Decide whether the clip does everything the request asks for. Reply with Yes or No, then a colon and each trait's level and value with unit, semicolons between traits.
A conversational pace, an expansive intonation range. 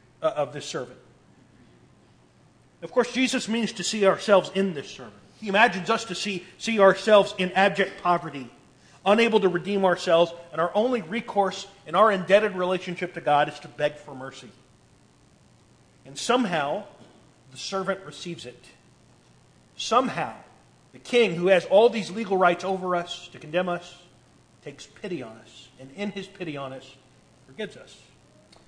Yes: average, 155 wpm; wide, 6.3 semitones